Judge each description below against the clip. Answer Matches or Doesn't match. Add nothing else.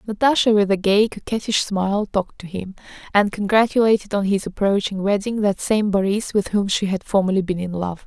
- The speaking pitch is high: Matches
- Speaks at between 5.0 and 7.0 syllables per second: Matches